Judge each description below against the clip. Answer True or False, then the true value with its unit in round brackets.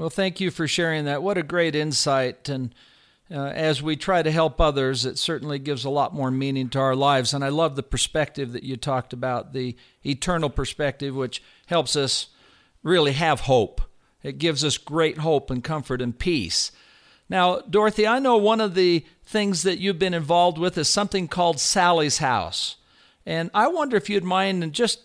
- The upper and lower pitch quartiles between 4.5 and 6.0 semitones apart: True (4.8 semitones)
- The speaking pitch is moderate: True (155 Hz)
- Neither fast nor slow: True (195 wpm)